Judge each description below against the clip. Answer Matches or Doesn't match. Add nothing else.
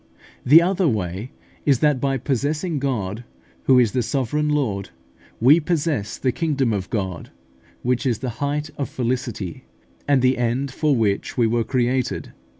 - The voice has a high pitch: Doesn't match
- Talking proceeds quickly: Doesn't match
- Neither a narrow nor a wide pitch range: Matches